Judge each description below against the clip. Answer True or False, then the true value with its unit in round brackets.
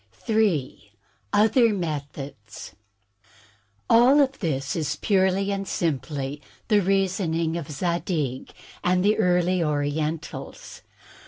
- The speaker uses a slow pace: True (100 wpm)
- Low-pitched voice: False (170 Hz)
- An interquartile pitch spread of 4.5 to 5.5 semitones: True (5.1 semitones)